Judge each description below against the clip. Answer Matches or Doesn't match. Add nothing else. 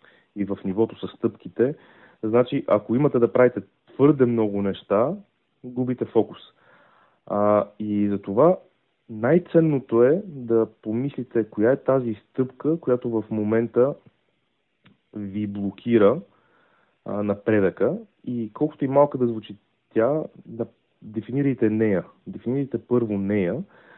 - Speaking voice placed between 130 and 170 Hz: Doesn't match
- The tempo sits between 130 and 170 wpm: Doesn't match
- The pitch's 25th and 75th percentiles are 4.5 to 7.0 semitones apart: Doesn't match